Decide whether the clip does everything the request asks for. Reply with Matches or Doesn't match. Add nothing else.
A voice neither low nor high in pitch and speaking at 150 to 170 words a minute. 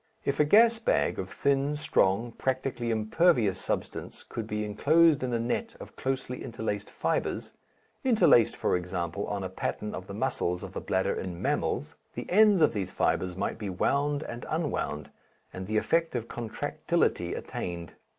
Doesn't match